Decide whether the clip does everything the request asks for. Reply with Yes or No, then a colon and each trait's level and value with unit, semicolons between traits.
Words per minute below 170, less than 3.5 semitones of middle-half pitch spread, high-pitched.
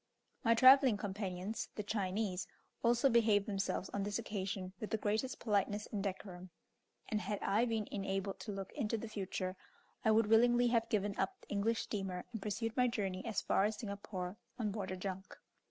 No: average, 185 wpm; narrow, 2.6 semitones; high, 205 Hz